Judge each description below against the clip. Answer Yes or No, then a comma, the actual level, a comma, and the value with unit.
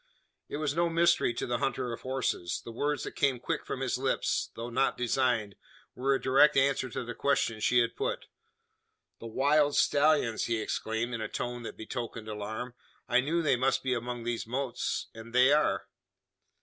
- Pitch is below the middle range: Yes, low, 125 Hz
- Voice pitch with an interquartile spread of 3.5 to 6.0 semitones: No, average, 3.0 semitones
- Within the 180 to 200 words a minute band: Yes, average, 190 wpm